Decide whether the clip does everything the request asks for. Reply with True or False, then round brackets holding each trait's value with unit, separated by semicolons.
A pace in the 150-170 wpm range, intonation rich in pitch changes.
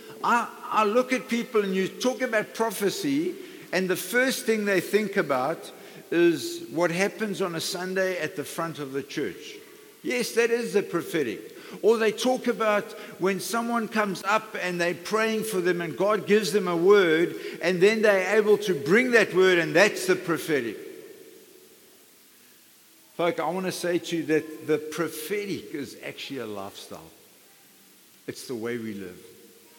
True (165 wpm; 5.7 semitones)